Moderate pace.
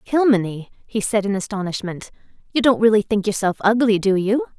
Yes: average, 170 wpm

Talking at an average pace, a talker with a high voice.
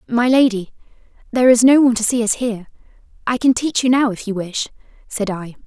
No: fast, 210 wpm; high, 230 Hz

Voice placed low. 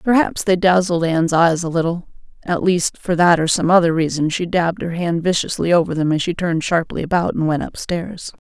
No: medium, 170 Hz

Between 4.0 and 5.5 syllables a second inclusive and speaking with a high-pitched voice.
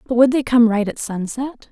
Yes: 5.2 syllables/s; high, 240 Hz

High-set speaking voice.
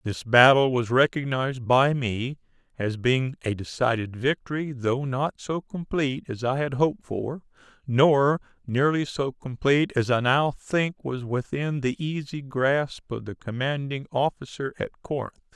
No: low, 135 Hz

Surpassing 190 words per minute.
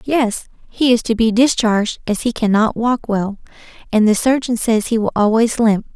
Yes: average, 200 wpm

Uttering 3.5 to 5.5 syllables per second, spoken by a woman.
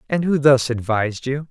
No: 5.3 syllables/s; male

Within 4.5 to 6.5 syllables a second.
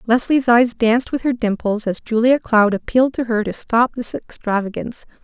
Yes: 5.3 syllables/s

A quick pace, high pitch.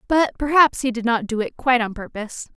Yes: fast, 230 wpm; high, 245 Hz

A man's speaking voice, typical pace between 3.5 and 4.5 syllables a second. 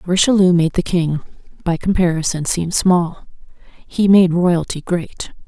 No: female; 4.2 syllables/s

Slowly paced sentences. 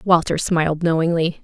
Yes: slow, 125 wpm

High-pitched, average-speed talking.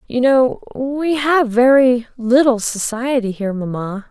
No: high, 245 Hz; slow, 130 wpm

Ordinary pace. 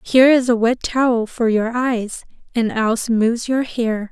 Yes: average, 190 wpm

